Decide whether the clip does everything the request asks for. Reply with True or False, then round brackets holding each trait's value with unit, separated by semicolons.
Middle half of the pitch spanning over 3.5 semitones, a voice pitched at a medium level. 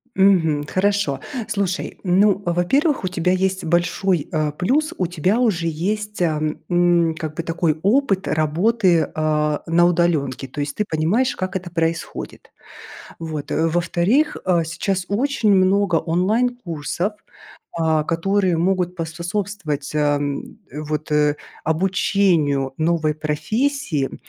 True (3.9 semitones; 175 Hz)